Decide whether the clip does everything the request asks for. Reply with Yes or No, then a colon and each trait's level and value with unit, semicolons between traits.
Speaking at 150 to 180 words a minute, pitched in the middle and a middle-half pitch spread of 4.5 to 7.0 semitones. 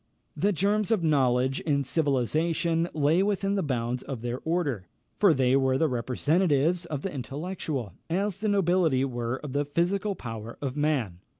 Yes: average, 165 wpm; medium, 150 Hz; wide, 5.4 semitones